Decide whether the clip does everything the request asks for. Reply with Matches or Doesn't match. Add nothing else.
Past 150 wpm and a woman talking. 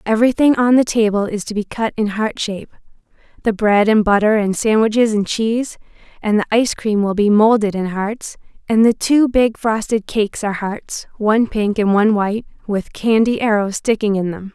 Matches